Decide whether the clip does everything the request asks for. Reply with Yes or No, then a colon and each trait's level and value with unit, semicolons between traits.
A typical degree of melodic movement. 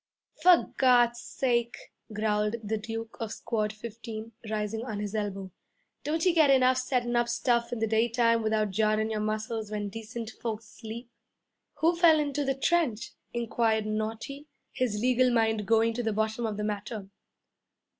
No: narrow, 2.2 semitones